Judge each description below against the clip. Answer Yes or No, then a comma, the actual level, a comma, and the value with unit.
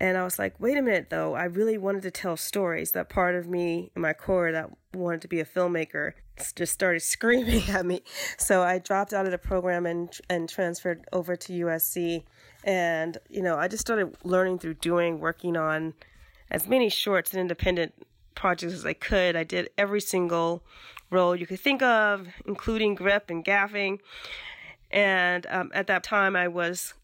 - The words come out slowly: No, average, 190 wpm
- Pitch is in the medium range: Yes, medium, 180 Hz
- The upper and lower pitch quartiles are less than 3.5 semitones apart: Yes, narrow, 2.5 semitones